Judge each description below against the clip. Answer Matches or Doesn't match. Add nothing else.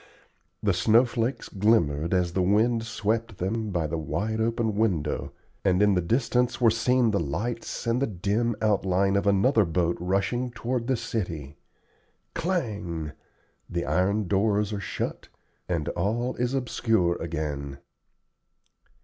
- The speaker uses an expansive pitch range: Doesn't match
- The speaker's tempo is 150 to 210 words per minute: Doesn't match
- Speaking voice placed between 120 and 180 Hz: Doesn't match